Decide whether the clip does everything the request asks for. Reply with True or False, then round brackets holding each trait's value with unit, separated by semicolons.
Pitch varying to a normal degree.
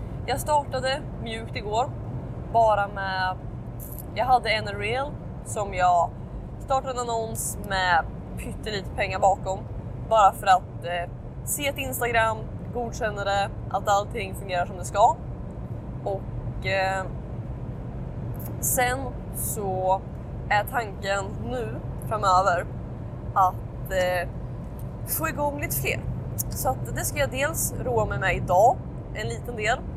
False (7.7 semitones)